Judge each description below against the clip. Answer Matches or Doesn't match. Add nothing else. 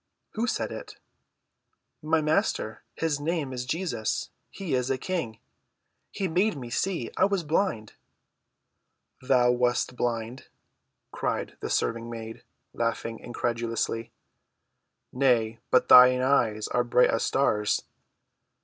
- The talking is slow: Matches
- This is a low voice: Matches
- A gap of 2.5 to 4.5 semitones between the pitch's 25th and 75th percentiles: Doesn't match